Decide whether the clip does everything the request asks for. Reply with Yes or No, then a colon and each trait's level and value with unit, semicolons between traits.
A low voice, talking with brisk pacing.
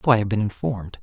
Yes: low, 105 Hz; fast, 295 wpm